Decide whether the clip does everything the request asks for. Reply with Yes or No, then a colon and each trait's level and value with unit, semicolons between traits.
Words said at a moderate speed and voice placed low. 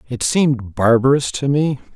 Yes: average, 155 wpm; low, 130 Hz